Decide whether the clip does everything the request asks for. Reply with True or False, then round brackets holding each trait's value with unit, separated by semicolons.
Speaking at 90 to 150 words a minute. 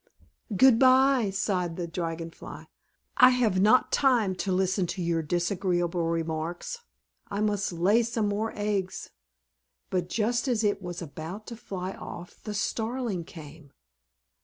True (140 wpm)